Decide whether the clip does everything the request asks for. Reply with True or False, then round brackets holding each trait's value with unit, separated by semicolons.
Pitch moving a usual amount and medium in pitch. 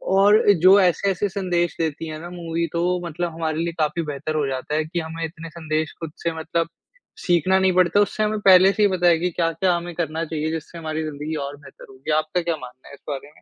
False (2.3 semitones; 165 Hz)